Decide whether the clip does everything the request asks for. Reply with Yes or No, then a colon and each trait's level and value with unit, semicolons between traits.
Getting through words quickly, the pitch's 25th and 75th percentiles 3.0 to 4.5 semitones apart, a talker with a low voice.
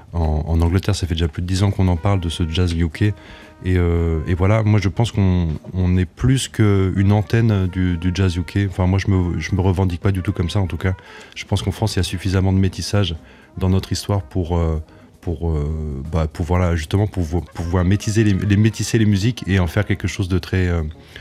No: fast, 235 wpm; narrow, 2.6 semitones; very low, 95 Hz